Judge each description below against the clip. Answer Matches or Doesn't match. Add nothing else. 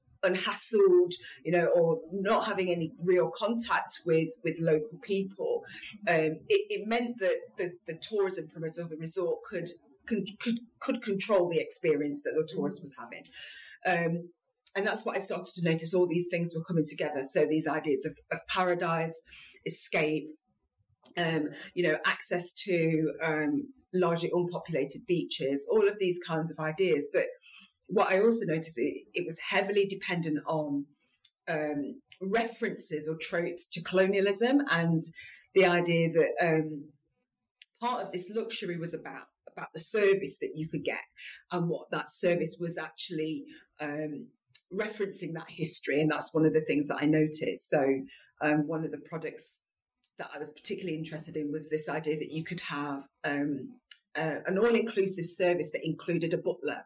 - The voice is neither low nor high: Matches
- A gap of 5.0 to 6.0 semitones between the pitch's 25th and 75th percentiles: Doesn't match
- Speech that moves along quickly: Doesn't match